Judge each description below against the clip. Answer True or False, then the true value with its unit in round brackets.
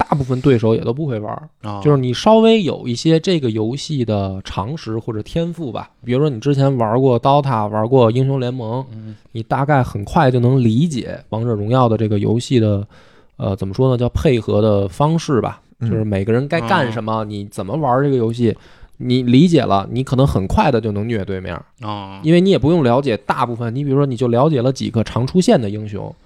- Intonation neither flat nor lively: True (4.4 semitones)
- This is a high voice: False (120 Hz)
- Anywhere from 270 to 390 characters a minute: True (320 characters per minute)